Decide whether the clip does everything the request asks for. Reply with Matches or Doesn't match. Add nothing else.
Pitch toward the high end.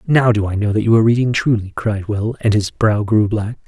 Doesn't match